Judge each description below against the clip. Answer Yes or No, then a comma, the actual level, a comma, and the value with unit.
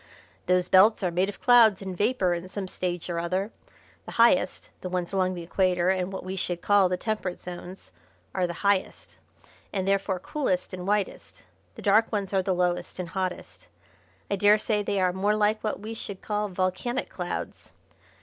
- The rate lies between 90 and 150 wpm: No, average, 185 wpm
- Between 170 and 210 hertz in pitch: Yes, high, 190 Hz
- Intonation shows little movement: Yes, narrow, 2.2 semitones